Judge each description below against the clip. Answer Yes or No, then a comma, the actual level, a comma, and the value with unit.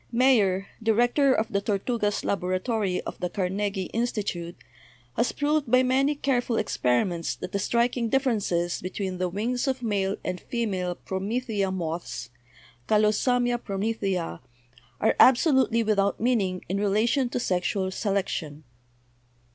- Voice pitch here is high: Yes, high, 210 Hz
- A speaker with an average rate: No, slow, 130 wpm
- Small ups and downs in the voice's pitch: No, average, 4.4 semitones